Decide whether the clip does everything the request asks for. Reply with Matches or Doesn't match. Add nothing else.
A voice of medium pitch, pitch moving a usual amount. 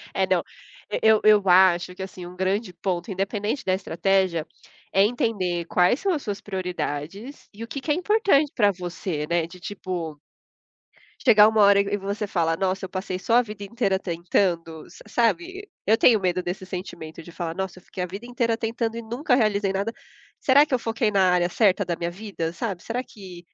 Doesn't match